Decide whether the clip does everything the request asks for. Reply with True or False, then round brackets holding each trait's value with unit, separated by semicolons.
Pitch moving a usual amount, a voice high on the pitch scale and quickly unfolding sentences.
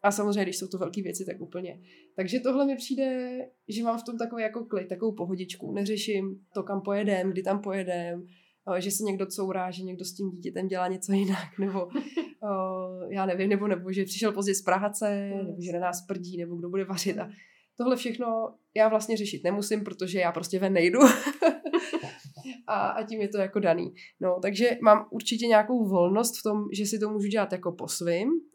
True (3.0 semitones; 195 Hz; 200 wpm)